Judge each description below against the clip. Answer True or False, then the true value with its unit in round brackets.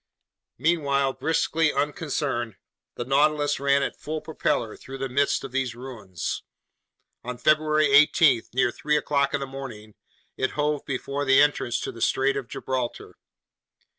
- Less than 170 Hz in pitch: True (140 Hz)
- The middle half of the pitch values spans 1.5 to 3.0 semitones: True (2.5 semitones)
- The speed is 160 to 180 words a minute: False (145 wpm)